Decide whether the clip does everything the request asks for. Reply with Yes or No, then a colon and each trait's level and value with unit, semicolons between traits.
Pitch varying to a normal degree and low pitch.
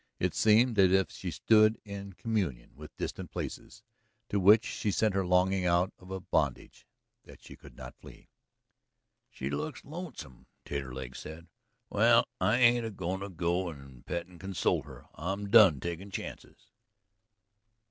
Yes: average, 3.6 semitones; very low, 95 Hz